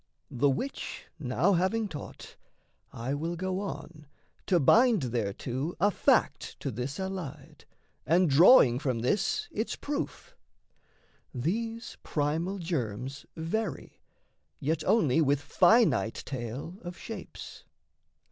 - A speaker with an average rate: No, slow, 110 wpm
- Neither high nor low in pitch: Yes, medium, 160 Hz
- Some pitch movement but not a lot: No, wide, 6.2 semitones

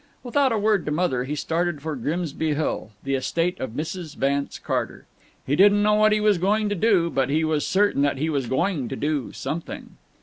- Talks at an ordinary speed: No, fast, 210 wpm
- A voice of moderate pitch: Yes, medium, 160 Hz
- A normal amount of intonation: No, wide, 6.1 semitones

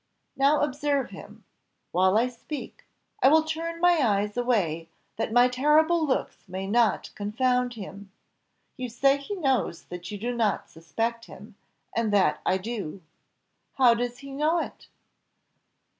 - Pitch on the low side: No, high, 245 Hz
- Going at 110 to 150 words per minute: Yes, average, 145 wpm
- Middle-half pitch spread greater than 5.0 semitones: Yes, wide, 5.4 semitones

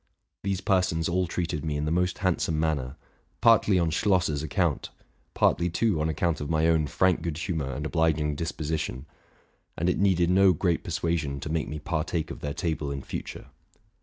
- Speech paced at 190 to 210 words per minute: Yes, average, 195 wpm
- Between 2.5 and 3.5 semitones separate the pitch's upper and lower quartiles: Yes, average, 2.8 semitones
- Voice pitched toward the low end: Yes, very low, 80 Hz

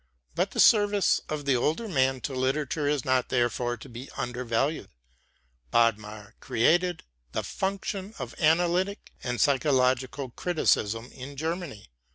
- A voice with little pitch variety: No, average, 5.1 semitones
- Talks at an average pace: No, slow, 130 wpm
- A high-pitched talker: No, low, 135 Hz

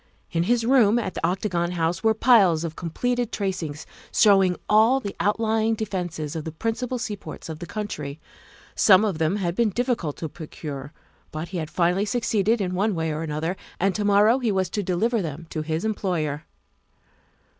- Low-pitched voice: No, high, 190 Hz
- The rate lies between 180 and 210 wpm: Yes, average, 185 wpm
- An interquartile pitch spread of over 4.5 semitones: Yes, average, 5.0 semitones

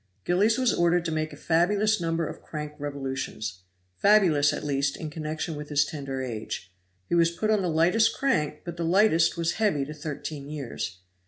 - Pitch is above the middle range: No, medium, 160 Hz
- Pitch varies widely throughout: No, average, 3.4 semitones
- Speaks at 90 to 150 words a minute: No, average, 185 wpm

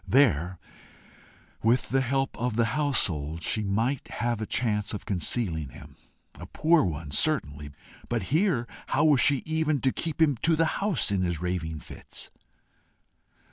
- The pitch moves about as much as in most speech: No, wide, 8.1 semitones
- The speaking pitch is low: Yes, low, 115 Hz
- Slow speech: No, average, 155 wpm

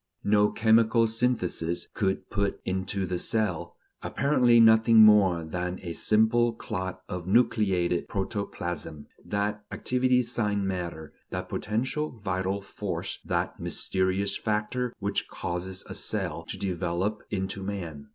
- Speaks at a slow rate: Yes, slow, 120 wpm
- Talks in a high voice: No, low, 100 Hz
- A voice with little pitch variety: No, average, 3.4 semitones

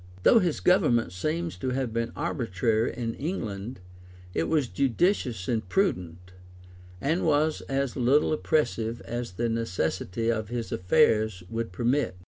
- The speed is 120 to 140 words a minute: Yes, slow, 135 wpm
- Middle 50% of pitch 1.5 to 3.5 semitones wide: No, average, 5.0 semitones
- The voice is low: Yes, low, 120 Hz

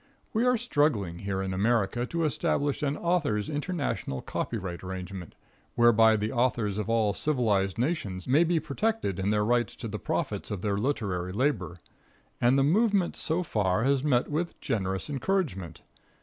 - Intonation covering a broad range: Yes, wide, 7.2 semitones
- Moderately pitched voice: No, low, 120 Hz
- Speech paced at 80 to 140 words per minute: No, average, 160 wpm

